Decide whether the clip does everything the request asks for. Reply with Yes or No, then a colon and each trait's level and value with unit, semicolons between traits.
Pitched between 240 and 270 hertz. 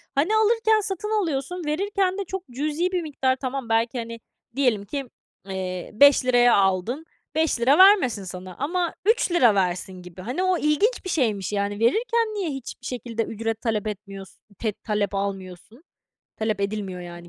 Yes: high, 245 Hz